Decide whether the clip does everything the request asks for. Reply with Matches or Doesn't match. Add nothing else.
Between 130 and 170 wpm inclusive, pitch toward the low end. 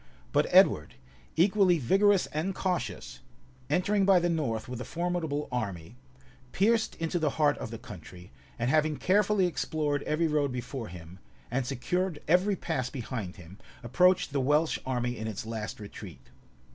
Doesn't match